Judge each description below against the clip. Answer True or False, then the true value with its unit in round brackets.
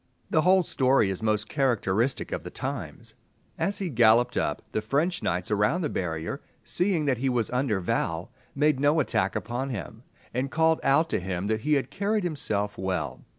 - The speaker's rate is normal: True (185 wpm)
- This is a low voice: True (125 Hz)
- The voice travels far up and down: True (6.6 semitones)